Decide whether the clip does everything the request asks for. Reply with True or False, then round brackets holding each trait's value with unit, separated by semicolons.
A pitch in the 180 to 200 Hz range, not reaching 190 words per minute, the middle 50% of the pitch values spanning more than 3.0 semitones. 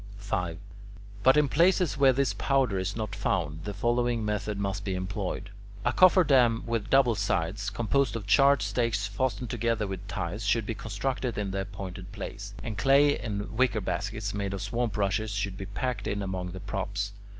False (105 Hz; 180 wpm; 3.5 semitones)